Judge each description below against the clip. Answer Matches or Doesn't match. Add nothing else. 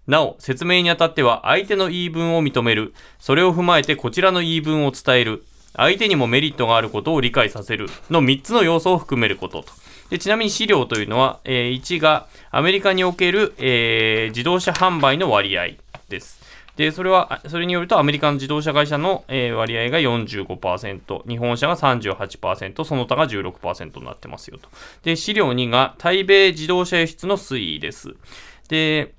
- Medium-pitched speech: Matches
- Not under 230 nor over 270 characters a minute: Doesn't match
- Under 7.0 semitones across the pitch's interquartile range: Matches